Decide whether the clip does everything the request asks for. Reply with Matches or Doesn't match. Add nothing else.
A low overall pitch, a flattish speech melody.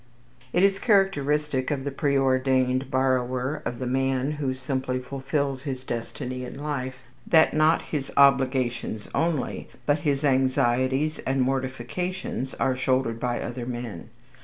Matches